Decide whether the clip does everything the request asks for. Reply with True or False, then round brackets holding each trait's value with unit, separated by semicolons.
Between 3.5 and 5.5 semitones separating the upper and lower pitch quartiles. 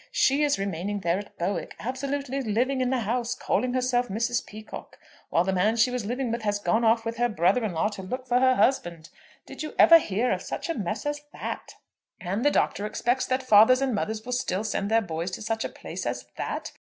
True (3.9 semitones)